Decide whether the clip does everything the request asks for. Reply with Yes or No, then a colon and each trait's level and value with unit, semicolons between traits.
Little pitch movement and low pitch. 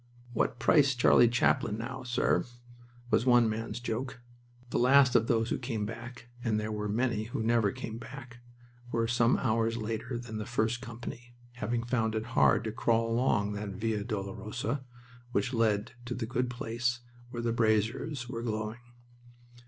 Yes: narrow, 1.8 semitones; low, 115 Hz